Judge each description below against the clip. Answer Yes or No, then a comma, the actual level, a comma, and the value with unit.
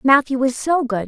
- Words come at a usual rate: No, fast, 220 wpm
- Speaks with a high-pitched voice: Yes, very high, 260 Hz